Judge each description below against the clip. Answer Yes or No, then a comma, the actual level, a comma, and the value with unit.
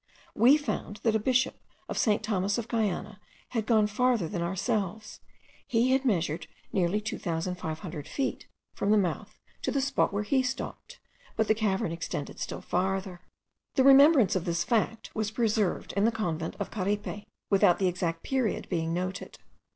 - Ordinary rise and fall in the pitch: Yes, average, 4.2 semitones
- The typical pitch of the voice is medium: No, high, 205 Hz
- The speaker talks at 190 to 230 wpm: No, average, 165 wpm